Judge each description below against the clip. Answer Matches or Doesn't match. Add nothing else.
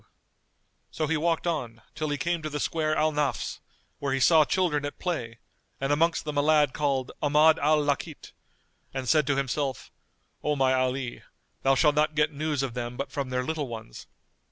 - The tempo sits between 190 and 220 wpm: Matches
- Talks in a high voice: Doesn't match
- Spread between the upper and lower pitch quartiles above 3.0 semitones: Doesn't match